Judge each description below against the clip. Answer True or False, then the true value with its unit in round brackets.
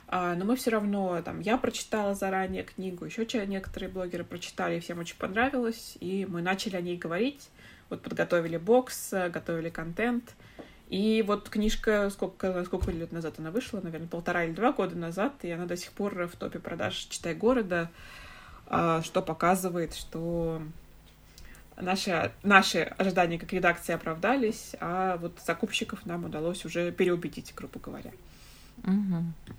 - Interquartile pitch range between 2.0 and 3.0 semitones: False (3.6 semitones)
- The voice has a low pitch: False (185 Hz)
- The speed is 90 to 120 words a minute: False (140 wpm)